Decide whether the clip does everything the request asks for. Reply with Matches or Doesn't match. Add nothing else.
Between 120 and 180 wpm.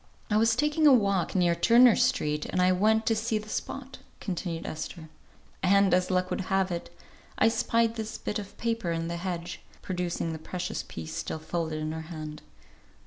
Doesn't match